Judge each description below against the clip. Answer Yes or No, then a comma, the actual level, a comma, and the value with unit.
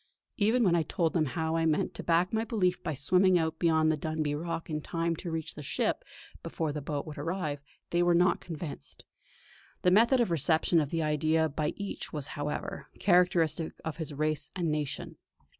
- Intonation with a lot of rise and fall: No, narrow, 2.5 semitones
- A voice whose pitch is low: No, medium, 160 Hz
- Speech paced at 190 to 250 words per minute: Yes, average, 195 wpm